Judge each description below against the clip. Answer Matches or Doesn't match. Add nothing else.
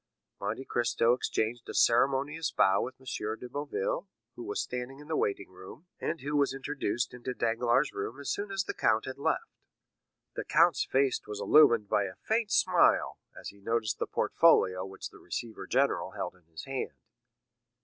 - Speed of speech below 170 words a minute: Doesn't match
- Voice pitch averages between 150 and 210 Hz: Doesn't match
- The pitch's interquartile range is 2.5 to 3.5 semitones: Doesn't match